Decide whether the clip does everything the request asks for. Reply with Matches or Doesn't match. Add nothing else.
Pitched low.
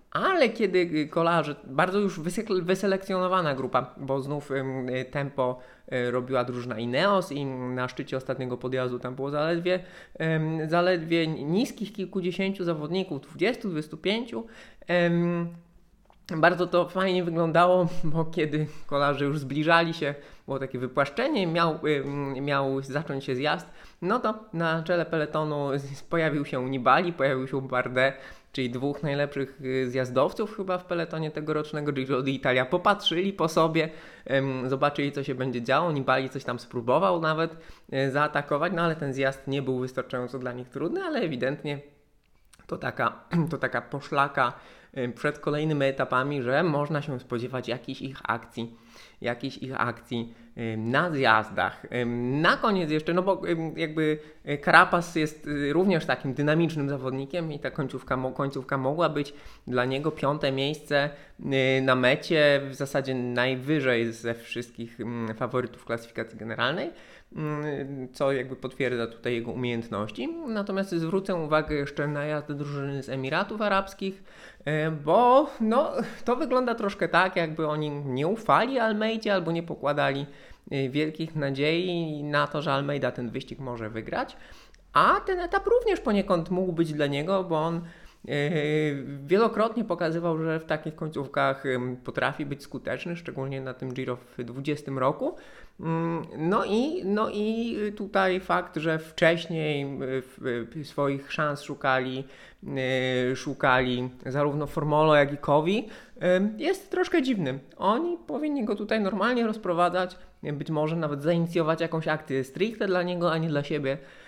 Doesn't match